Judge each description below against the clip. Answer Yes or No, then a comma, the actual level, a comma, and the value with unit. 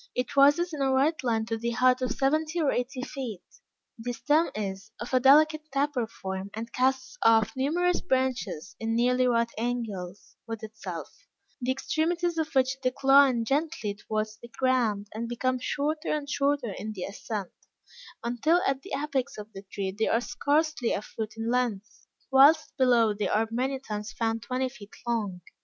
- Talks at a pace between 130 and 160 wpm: No, average, 175 wpm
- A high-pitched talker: Yes, very high, 250 Hz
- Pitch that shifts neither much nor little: Yes, average, 3.9 semitones